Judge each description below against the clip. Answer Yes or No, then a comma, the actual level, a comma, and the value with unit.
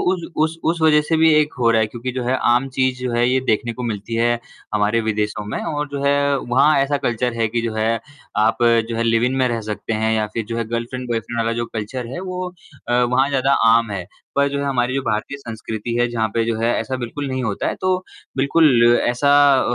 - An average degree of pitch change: Yes, average, 3.2 semitones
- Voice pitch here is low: Yes, low, 120 Hz